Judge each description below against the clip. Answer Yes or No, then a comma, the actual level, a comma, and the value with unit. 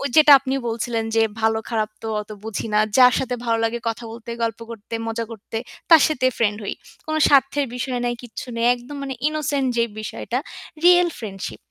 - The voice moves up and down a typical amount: Yes, average, 3.3 semitones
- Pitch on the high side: Yes, high, 235 Hz